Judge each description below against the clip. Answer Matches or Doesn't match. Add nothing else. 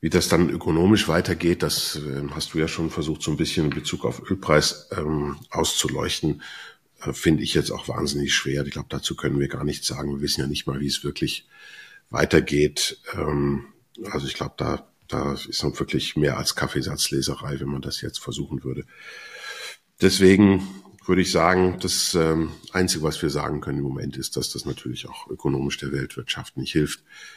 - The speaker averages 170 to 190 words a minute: Matches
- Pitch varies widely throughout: Doesn't match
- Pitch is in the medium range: Doesn't match